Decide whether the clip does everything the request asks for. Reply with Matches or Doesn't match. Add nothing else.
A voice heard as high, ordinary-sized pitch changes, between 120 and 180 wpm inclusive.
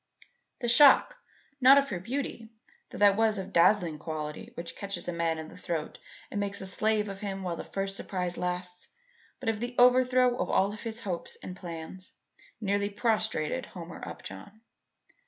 Matches